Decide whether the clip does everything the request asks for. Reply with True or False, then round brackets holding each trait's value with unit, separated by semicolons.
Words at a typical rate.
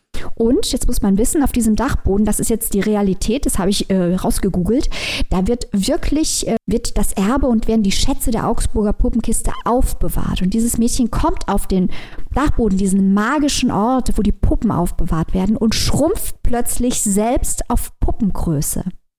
True (170 wpm)